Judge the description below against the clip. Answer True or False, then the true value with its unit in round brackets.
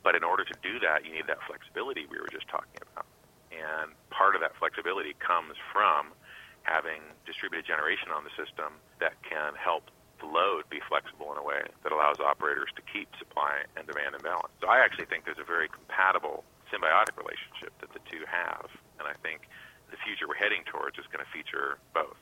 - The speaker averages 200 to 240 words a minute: True (205 wpm)